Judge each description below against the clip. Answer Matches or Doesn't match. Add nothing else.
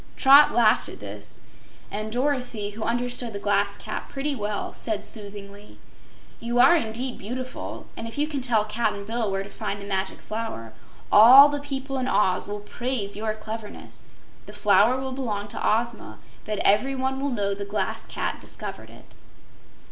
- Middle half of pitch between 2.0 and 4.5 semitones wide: Matches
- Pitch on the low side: Doesn't match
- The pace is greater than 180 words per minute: Doesn't match